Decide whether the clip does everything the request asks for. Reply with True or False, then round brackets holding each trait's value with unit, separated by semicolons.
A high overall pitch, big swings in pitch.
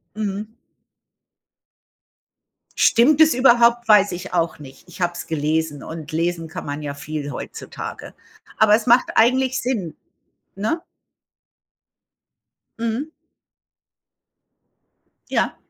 True (200 Hz; 6.8 semitones)